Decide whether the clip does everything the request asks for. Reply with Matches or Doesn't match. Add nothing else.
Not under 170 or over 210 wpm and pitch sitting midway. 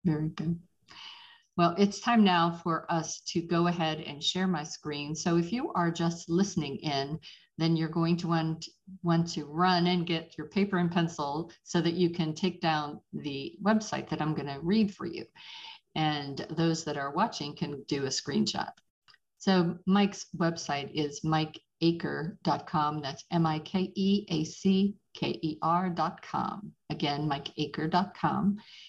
Doesn't match